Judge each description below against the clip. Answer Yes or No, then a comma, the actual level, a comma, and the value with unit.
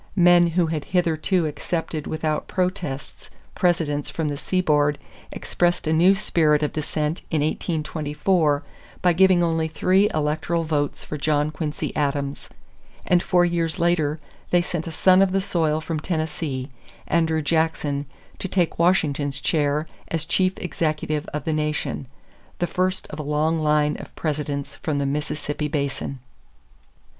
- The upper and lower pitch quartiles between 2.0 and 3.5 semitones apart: Yes, average, 2.7 semitones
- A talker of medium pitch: Yes, medium, 155 Hz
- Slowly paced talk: No, average, 145 wpm